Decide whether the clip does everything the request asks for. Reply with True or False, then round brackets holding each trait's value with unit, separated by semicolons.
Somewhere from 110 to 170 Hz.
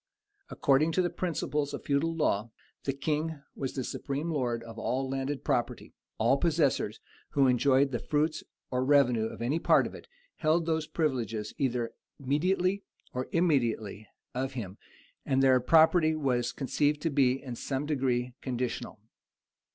True (135 Hz)